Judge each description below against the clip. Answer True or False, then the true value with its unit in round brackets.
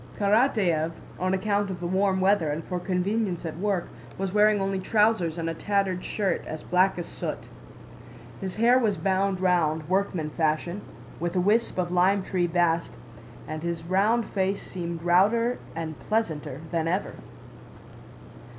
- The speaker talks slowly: False (155 wpm)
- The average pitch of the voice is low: False (185 Hz)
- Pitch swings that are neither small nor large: True (3.0 semitones)